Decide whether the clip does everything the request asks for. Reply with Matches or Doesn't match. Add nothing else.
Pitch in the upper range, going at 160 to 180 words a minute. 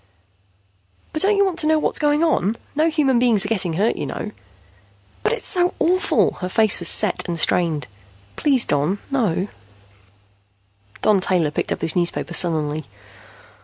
Matches